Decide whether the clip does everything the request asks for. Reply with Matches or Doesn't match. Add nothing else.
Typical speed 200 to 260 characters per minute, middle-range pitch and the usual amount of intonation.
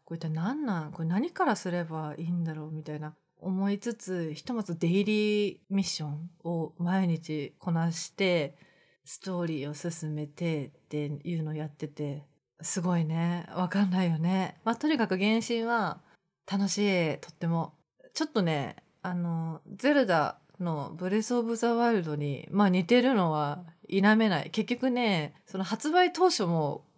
Doesn't match